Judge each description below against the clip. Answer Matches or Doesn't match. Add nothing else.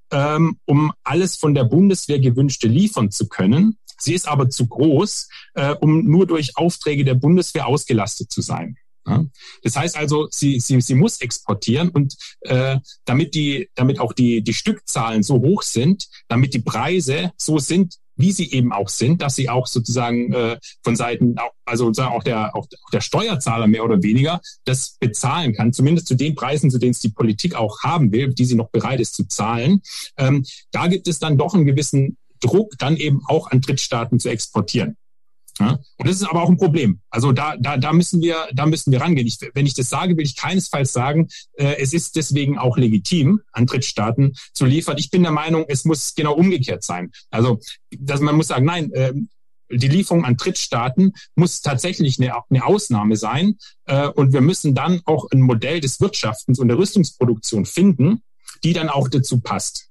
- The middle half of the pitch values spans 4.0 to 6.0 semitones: Matches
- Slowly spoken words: Doesn't match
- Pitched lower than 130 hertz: Doesn't match